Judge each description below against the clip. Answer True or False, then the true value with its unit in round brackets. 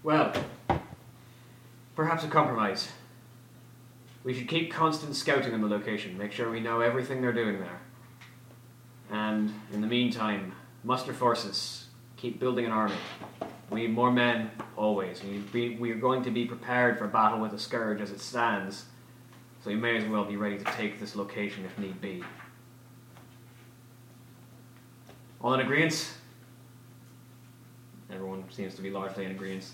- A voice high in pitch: False (120 Hz)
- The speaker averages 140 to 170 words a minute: True (150 wpm)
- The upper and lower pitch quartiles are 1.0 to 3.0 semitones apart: True (2.6 semitones)